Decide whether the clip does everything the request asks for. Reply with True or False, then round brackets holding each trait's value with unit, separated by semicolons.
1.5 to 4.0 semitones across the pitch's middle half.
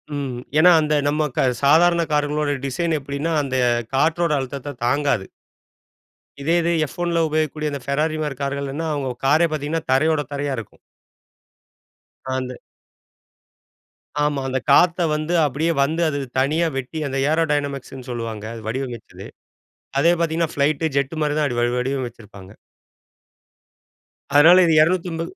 True (3.1 semitones)